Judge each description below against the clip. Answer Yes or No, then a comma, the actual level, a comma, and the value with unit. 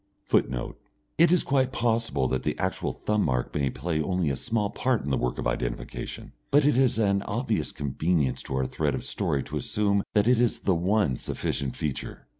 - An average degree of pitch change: No, wide, 9.0 semitones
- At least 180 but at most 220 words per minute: Yes, average, 200 wpm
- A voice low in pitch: Yes, low, 100 Hz